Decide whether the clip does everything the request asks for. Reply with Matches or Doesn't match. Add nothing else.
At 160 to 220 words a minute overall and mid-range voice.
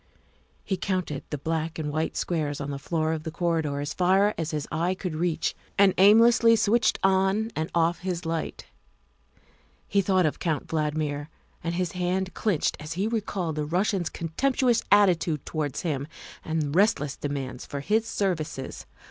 Matches